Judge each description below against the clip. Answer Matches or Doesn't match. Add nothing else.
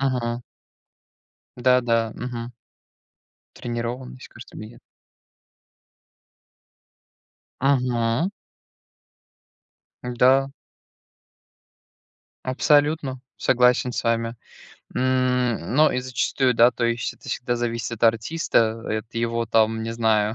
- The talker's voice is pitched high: Doesn't match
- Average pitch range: Doesn't match